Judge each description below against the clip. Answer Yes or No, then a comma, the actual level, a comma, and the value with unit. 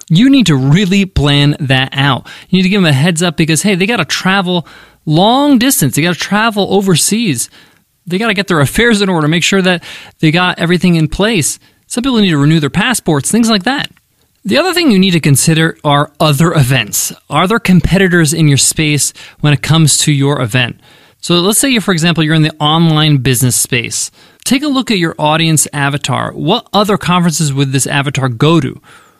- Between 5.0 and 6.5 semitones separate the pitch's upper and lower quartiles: Yes, average, 5.3 semitones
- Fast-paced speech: Yes, fast, 210 wpm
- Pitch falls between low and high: Yes, medium, 165 Hz